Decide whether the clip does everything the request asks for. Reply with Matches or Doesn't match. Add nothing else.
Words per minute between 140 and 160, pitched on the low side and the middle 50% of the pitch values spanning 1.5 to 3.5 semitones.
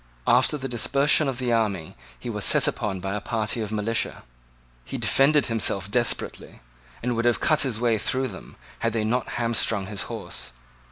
Doesn't match